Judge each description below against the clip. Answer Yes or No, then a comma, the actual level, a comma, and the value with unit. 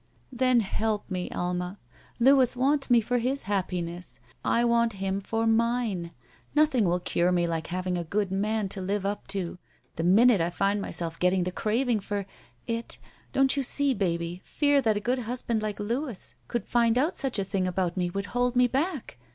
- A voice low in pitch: No, high, 210 Hz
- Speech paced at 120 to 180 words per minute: No, average, 195 wpm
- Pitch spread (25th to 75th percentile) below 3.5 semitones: No, average, 5.1 semitones